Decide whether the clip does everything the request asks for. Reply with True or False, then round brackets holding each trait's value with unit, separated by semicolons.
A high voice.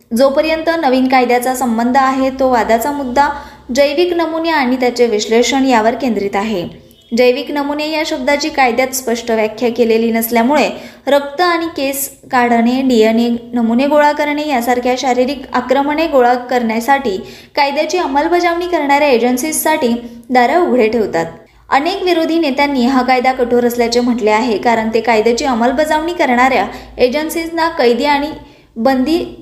True (260 Hz)